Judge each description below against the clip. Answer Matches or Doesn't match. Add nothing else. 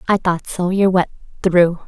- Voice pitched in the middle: Matches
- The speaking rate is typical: Matches